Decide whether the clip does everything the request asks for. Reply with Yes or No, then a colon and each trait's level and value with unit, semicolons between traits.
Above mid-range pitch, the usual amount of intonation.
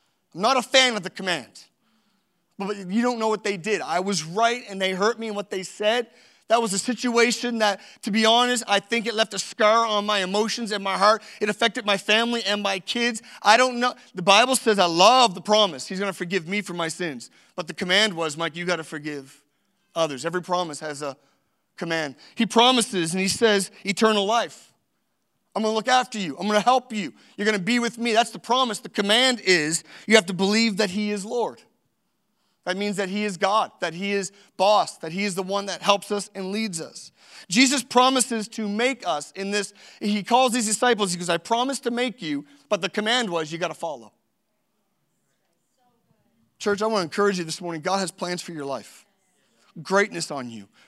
Yes: high, 205 Hz; average, 3.9 semitones